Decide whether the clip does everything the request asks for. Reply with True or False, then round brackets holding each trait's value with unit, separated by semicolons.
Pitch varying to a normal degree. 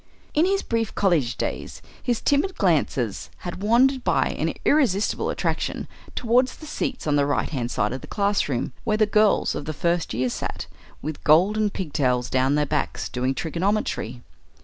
False (8.2 semitones)